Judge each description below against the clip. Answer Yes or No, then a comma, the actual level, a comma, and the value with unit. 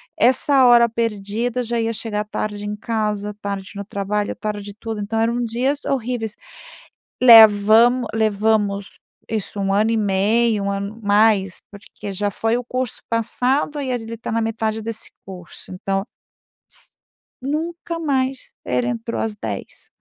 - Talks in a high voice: Yes, high, 220 Hz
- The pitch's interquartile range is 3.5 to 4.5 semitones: No, average, 2.7 semitones